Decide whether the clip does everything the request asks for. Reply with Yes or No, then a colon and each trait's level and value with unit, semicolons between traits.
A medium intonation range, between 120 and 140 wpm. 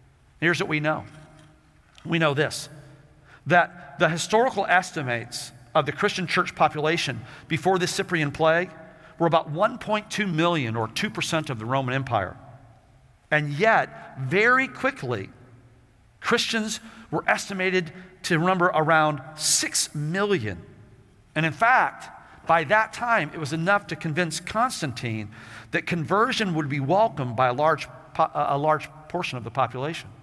Yes: average, 4.9 semitones; slow, 135 wpm